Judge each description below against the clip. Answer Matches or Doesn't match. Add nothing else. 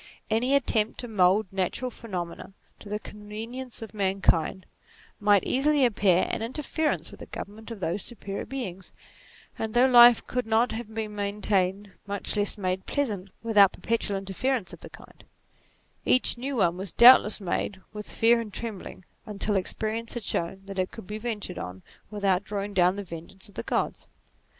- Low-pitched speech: Doesn't match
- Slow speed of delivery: Doesn't match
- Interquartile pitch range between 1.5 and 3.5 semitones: Matches